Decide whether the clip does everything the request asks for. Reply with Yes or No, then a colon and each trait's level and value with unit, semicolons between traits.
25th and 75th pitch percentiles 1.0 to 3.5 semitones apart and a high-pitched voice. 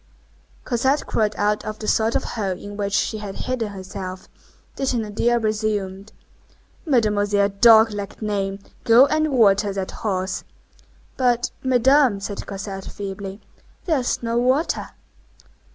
Yes: average, 3.2 semitones; high, 215 Hz